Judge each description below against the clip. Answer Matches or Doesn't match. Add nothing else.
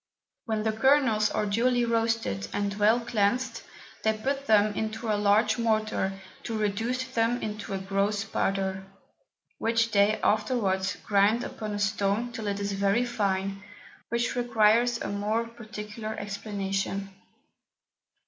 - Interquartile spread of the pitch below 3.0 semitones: Matches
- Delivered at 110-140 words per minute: Matches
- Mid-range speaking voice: Doesn't match